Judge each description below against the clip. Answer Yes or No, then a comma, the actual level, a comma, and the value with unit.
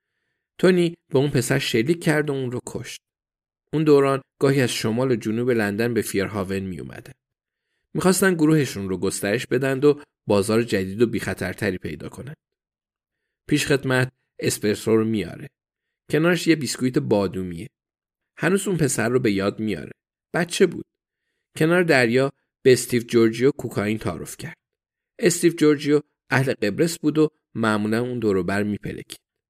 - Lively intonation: Yes, wide, 6.1 semitones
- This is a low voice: Yes, low, 125 Hz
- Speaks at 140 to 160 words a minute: Yes, average, 145 wpm